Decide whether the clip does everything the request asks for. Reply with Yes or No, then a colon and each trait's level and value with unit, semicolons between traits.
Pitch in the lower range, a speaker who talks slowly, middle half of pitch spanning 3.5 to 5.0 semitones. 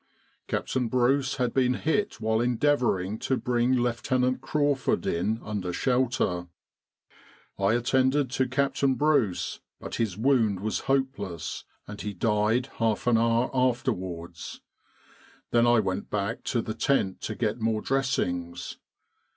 Yes: low, 120 Hz; slow, 130 wpm; average, 3.8 semitones